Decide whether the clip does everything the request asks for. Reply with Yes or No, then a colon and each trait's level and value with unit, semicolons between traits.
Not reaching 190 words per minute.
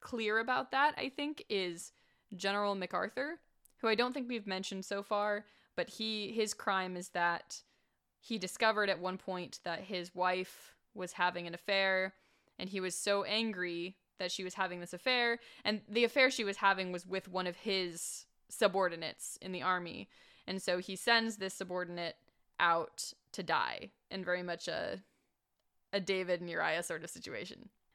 Yes: average, 170 wpm